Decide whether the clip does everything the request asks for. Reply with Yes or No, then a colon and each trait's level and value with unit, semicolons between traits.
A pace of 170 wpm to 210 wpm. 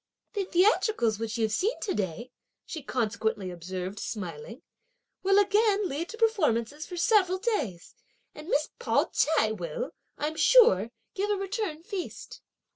No: average, 140 wpm